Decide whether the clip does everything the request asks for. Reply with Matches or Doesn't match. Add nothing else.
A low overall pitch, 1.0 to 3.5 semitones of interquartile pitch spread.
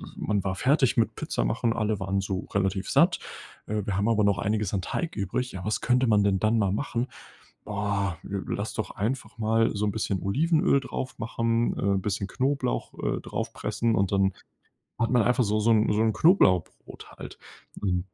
Matches